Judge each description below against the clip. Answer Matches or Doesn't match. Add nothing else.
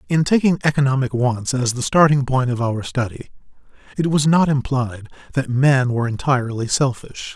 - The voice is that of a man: Matches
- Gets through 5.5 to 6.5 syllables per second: Doesn't match